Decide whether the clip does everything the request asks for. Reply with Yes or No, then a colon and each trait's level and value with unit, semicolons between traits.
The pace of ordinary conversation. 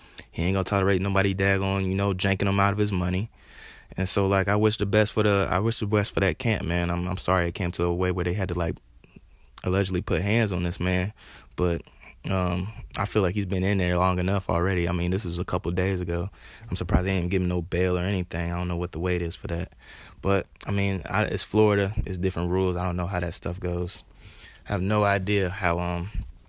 No: fast, 250 wpm